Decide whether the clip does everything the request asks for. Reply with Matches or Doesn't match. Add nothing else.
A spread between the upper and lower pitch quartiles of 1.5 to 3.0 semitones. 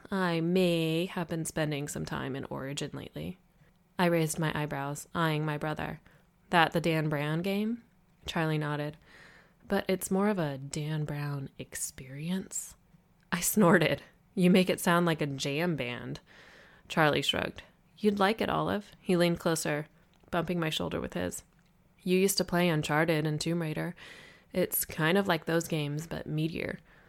Matches